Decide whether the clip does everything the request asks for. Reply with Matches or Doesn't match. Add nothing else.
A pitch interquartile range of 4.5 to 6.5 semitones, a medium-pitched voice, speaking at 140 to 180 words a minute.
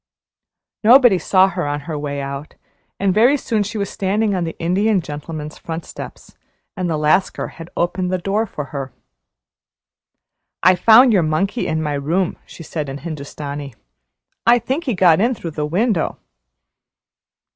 Matches